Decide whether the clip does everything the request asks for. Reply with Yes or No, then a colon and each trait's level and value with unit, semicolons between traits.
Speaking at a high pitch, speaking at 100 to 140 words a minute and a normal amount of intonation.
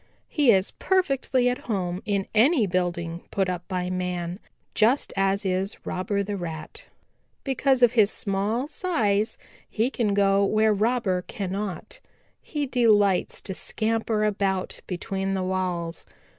Yes: high, 200 Hz; slow, 135 wpm; average, 3.6 semitones